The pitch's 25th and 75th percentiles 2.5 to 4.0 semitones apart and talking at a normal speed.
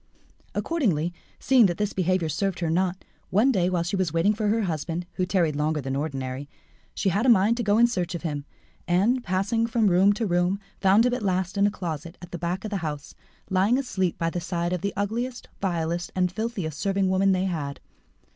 No: average, 3.3 semitones; fast, 215 wpm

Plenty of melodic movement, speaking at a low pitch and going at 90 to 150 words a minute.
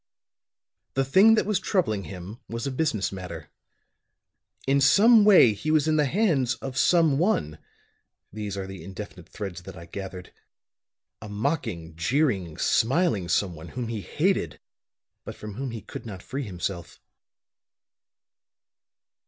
Yes: wide, 7.8 semitones; low, 110 Hz; average, 140 wpm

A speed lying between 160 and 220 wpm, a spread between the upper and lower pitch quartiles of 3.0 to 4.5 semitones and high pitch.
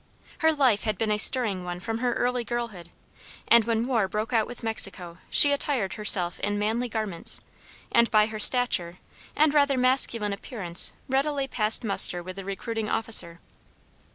Yes: average, 165 wpm; average, 3.9 semitones; high, 220 Hz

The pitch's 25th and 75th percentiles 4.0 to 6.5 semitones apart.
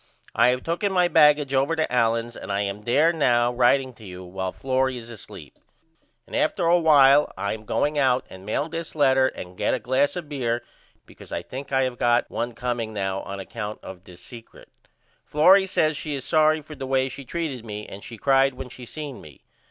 Yes: average, 4.4 semitones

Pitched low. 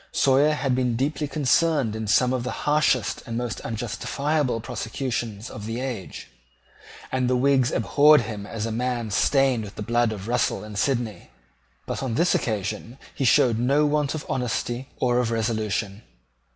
Yes: low, 125 Hz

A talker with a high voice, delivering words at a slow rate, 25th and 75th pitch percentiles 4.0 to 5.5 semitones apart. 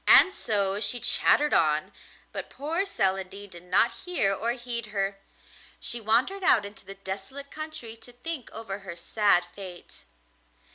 No: high, 215 Hz; average, 150 wpm; average, 4.3 semitones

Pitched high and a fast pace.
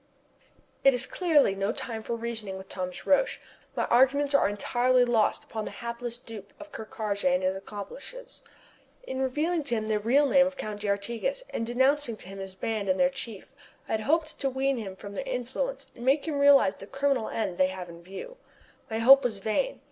Yes: high, 235 Hz; fast, 210 wpm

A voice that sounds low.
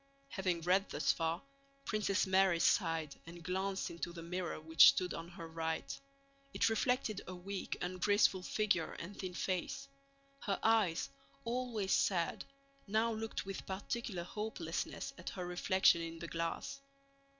No: medium, 185 Hz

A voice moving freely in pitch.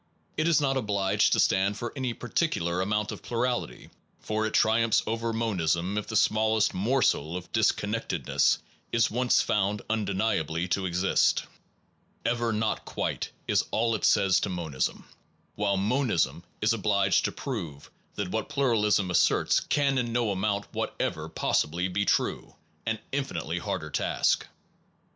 No: average, 3.5 semitones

